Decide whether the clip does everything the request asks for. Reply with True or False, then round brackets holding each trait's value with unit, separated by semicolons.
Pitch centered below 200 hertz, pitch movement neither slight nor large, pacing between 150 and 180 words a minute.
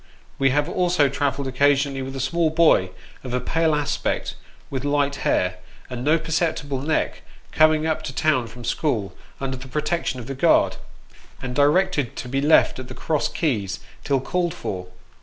True (140 Hz; 3.4 semitones; 175 wpm)